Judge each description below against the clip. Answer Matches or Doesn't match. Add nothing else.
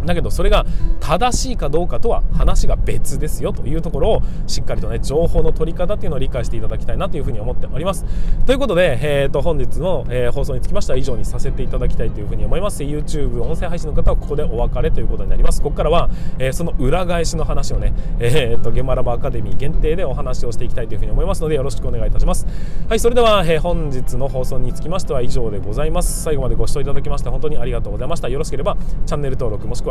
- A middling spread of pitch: Matches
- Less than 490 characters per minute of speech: Doesn't match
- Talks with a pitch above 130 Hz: Matches